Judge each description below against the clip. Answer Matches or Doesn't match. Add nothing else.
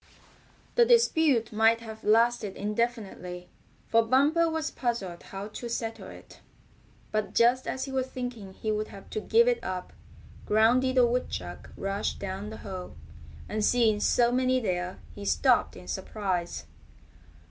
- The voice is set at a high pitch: Matches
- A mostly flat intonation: Doesn't match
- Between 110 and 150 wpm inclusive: Matches